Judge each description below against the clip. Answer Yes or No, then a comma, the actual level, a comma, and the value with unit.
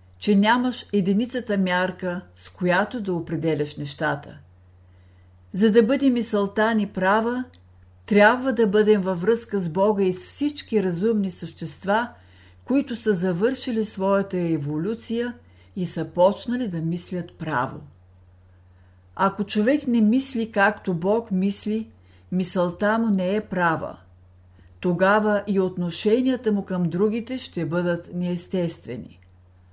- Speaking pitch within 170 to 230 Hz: Yes, medium, 185 Hz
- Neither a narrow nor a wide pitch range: No, wide, 5.9 semitones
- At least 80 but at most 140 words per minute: Yes, average, 120 wpm